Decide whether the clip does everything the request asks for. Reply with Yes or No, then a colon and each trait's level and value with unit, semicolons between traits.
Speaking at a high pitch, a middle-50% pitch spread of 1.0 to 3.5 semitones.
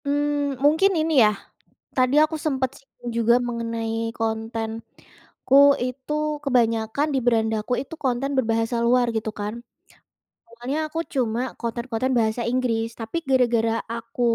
Yes: high, 240 Hz; average, 2.9 semitones